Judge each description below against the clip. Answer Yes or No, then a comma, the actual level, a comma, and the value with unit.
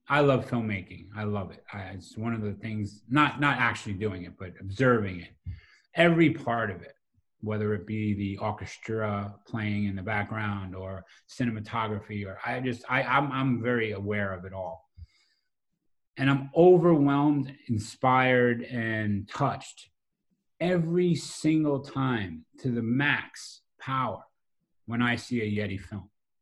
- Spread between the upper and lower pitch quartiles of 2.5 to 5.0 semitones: Yes, average, 4.6 semitones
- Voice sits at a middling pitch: No, low, 110 Hz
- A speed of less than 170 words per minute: Yes, average, 140 wpm